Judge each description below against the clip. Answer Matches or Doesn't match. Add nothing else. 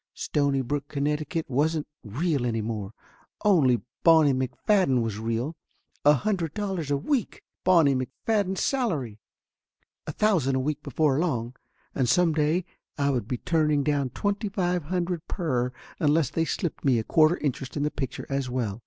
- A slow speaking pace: Doesn't match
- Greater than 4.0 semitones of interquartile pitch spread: Matches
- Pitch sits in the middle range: Matches